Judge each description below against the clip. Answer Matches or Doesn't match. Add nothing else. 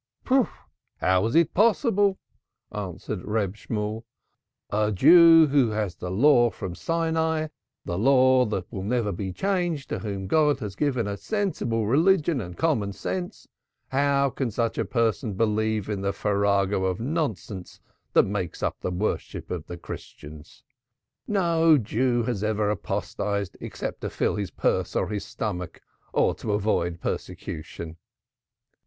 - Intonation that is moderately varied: Doesn't match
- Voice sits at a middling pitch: Doesn't match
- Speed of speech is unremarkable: Matches